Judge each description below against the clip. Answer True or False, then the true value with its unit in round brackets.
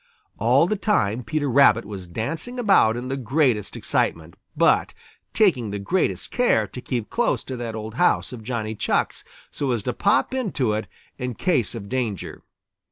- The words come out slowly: False (170 wpm)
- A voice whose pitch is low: True (125 Hz)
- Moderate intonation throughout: False (6.0 semitones)